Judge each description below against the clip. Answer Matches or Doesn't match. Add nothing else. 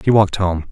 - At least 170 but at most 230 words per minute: Doesn't match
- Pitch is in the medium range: Doesn't match